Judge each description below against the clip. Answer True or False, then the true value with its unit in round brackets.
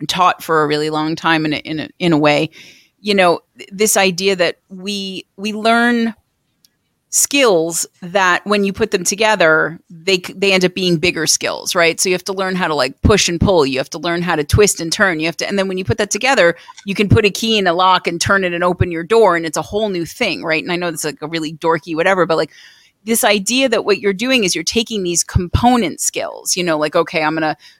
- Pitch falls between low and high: True (180 Hz)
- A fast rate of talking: True (255 wpm)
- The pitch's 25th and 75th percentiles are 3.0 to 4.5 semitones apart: True (3.7 semitones)